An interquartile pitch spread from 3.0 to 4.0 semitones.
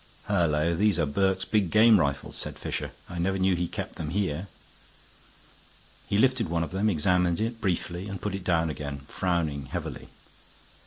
Yes: average, 3.4 semitones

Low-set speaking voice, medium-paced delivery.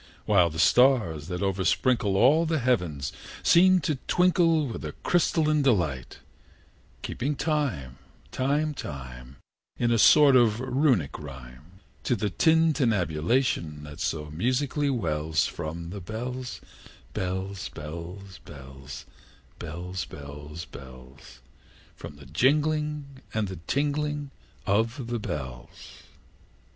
No: low, 100 Hz; slow, 110 wpm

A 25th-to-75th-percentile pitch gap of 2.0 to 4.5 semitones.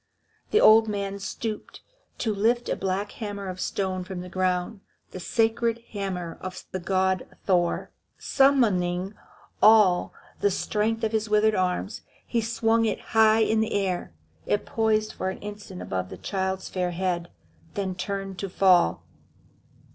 Yes: average, 2.9 semitones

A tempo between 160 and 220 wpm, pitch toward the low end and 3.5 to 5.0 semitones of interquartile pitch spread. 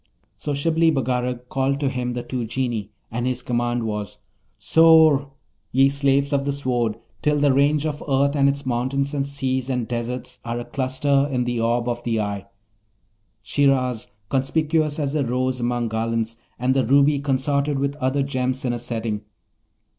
No: average, 170 wpm; low, 130 Hz; average, 2.7 semitones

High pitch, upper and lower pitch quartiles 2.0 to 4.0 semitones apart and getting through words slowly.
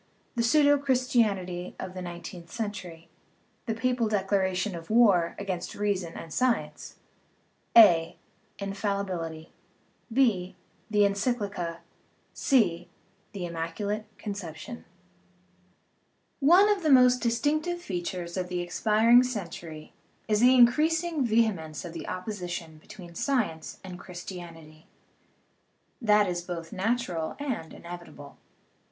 No: high, 195 Hz; average, 5.3 semitones; slow, 110 wpm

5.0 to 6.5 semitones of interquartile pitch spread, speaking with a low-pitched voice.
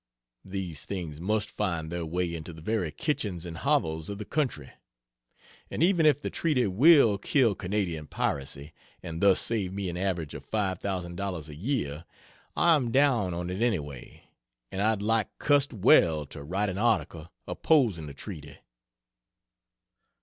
Yes: average, 5.3 semitones; very low, 95 Hz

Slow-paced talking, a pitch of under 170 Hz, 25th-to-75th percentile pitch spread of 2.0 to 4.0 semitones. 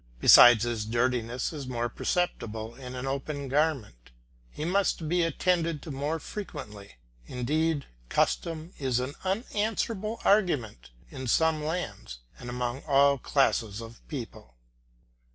No: slow, 125 wpm; low, 135 Hz; wide, 5.4 semitones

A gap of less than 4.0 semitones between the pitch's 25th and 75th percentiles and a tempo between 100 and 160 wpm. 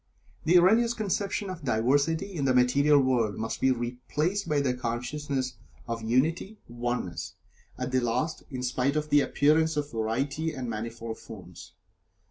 No: average, 4.6 semitones; average, 150 wpm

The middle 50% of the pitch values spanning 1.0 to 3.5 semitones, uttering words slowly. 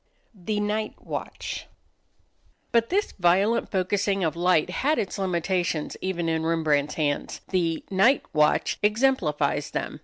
No: average, 4.3 semitones; slow, 130 wpm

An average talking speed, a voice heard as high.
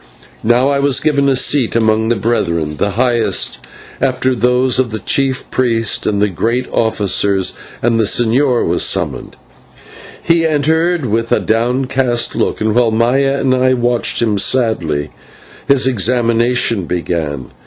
No: average, 150 wpm; low, 120 Hz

